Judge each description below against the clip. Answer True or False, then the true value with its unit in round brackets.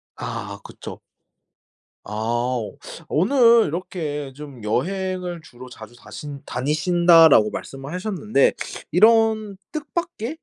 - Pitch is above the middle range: False (165 Hz)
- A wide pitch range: True (7.5 semitones)